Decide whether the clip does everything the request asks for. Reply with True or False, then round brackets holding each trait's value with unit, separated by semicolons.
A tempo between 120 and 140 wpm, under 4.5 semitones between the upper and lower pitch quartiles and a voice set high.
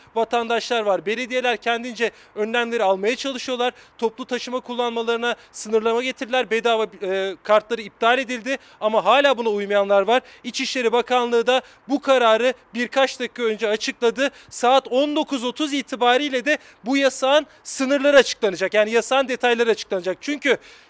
True (125 wpm; 2.6 semitones; 240 Hz)